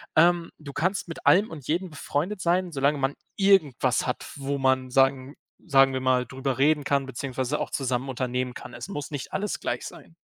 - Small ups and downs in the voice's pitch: No, average, 4.0 semitones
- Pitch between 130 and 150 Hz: Yes, medium, 140 Hz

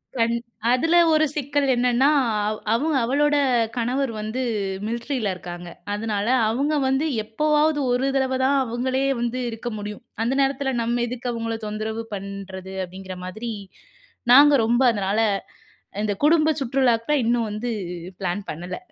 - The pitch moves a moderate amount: Yes, average, 4.2 semitones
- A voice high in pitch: Yes, high, 240 Hz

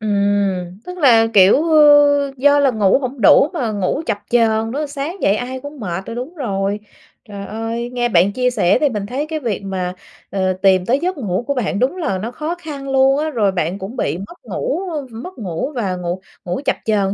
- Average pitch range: No, wide, 6.3 semitones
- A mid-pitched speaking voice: No, high, 235 Hz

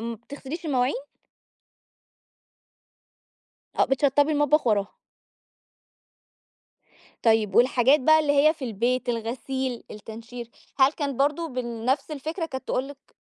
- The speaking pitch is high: Yes, very high, 265 Hz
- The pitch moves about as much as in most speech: Yes, average, 3.5 semitones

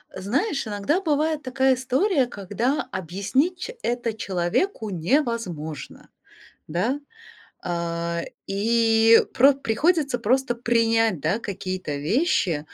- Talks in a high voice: Yes, high, 230 Hz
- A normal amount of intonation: No, wide, 6.4 semitones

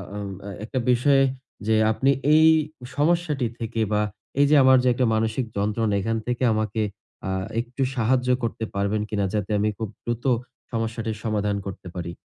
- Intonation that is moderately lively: Yes, average, 3.1 semitones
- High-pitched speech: No, low, 115 Hz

